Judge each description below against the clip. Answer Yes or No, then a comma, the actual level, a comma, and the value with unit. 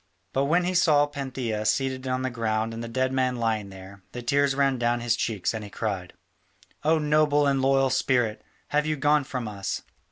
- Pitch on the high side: No, low, 130 Hz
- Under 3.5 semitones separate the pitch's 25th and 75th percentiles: No, average, 3.9 semitones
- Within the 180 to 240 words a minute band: Yes, average, 200 wpm